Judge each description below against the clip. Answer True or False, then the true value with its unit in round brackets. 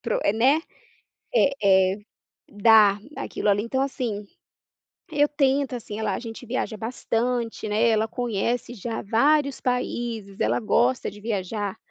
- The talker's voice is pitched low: False (225 Hz)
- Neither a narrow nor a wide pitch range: True (3.2 semitones)